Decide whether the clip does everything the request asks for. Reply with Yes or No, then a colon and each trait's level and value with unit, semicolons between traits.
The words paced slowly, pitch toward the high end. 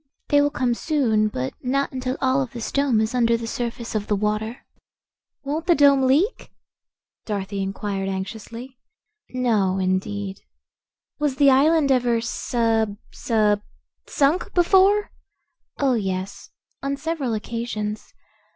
Yes: slow, 130 wpm; high, 235 Hz